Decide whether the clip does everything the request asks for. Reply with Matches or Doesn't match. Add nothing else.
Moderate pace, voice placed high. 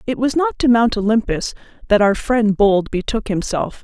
Matches